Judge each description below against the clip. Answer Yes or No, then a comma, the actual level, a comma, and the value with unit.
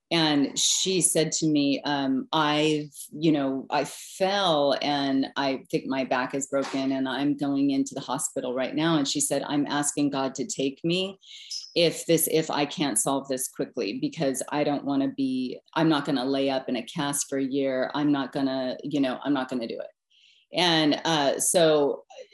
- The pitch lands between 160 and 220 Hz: No, medium, 140 Hz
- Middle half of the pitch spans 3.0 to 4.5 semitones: No, narrow, 2.5 semitones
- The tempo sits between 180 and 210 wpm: Yes, fast, 205 wpm